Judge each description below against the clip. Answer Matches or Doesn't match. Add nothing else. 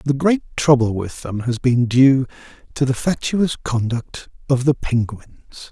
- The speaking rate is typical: Matches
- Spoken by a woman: Doesn't match